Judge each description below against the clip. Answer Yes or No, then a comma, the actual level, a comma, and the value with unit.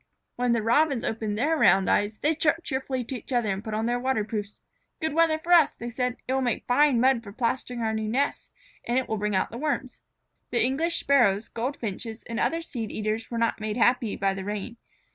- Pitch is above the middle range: Yes, high, 240 Hz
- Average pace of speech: No, fast, 220 wpm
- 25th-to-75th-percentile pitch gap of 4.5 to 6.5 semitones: No, average, 3.6 semitones